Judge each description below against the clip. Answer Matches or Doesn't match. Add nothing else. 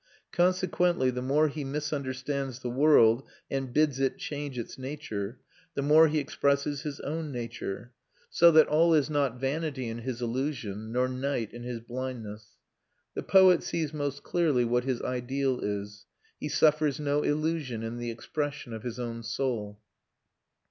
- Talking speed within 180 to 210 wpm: Doesn't match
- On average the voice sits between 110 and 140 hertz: Matches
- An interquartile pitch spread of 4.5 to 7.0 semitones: Doesn't match